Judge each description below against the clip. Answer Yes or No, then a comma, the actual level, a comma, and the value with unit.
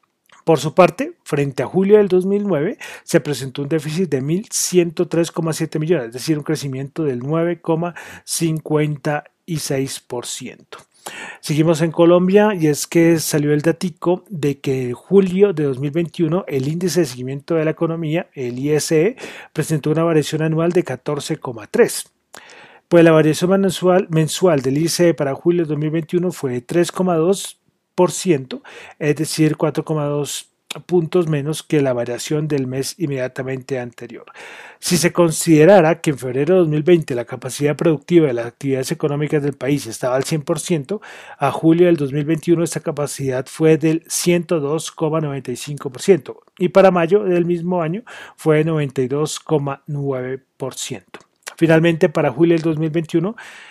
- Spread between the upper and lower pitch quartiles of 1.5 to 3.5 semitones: Yes, average, 3.1 semitones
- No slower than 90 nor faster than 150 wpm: Yes, average, 135 wpm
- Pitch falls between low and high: Yes, medium, 160 Hz